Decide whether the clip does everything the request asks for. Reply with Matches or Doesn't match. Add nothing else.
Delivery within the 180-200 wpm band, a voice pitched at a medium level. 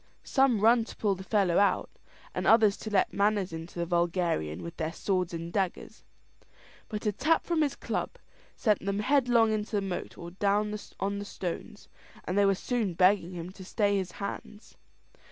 Doesn't match